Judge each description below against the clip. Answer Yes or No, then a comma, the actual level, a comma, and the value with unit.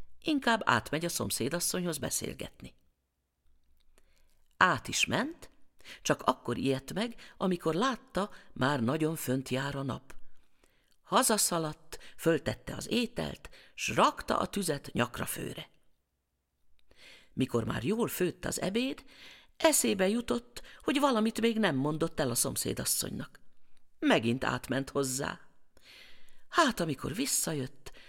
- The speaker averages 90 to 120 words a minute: Yes, average, 110 wpm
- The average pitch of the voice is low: No, medium, 150 Hz